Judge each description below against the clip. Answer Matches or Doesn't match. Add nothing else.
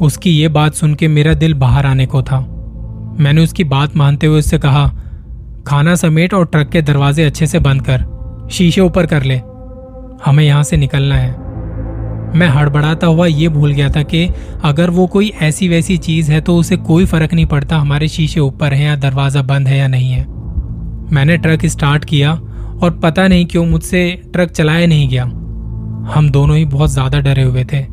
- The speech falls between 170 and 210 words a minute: Matches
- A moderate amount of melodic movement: Matches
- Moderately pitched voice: Matches